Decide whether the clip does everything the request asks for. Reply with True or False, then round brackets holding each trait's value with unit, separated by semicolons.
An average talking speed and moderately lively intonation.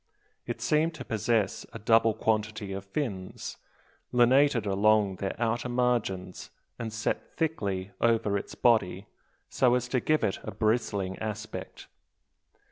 False (130 wpm; 3.5 semitones)